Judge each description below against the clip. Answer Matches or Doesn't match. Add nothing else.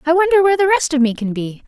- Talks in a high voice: Matches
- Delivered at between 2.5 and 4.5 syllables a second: Doesn't match